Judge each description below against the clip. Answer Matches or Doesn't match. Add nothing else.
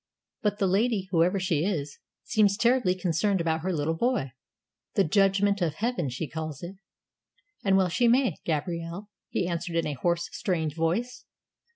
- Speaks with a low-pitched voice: Doesn't match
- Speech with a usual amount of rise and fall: Matches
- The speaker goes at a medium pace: Matches